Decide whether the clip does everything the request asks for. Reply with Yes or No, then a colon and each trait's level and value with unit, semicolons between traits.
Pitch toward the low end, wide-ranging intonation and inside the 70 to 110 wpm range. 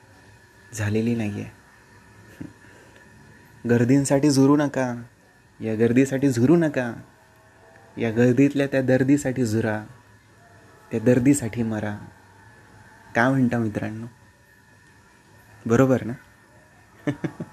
No: low, 115 Hz; average, 3.1 semitones; slow, 80 wpm